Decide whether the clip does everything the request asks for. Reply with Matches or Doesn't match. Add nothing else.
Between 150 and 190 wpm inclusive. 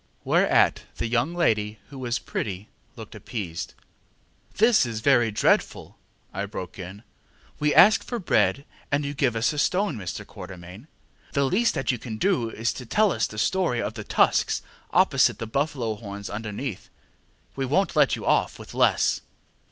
Matches